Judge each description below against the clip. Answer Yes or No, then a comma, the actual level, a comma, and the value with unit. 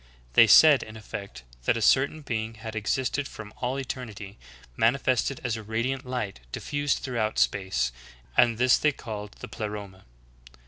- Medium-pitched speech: No, low, 115 Hz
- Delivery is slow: No, average, 150 wpm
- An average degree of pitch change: Yes, average, 3.5 semitones